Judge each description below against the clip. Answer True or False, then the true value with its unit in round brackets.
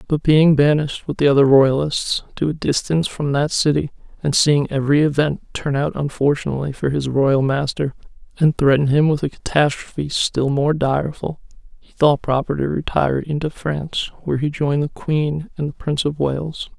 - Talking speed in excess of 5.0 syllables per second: True (5.3 syllables/s)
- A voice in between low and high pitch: True (145 Hz)